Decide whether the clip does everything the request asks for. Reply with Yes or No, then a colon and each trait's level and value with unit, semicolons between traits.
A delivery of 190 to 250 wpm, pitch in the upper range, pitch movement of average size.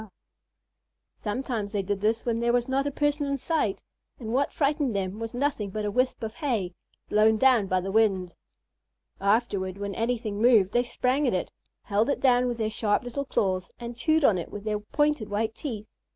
Yes: average, 195 wpm; high, 225 Hz; average, 3.9 semitones